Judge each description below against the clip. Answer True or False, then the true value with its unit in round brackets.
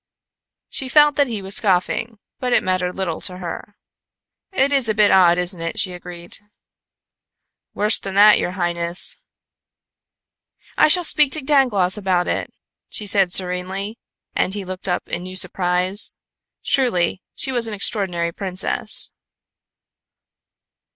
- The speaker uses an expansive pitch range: False (3.7 semitones)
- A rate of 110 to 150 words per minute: True (140 wpm)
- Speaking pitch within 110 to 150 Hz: False (190 Hz)